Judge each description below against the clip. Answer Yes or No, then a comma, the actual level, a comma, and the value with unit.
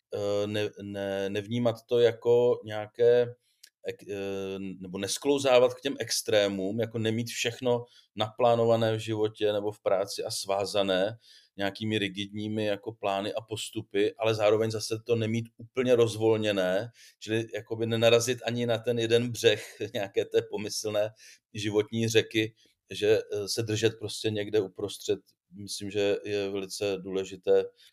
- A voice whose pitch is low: Yes, low, 110 Hz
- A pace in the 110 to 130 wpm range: Yes, average, 125 wpm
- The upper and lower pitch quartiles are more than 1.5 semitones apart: Yes, narrow, 2.4 semitones